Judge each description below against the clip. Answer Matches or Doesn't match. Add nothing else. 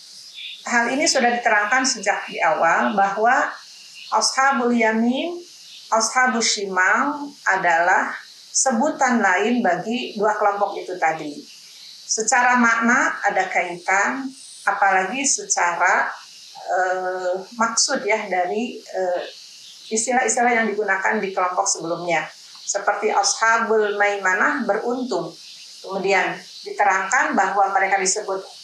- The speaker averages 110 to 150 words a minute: Doesn't match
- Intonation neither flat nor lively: Matches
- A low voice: Doesn't match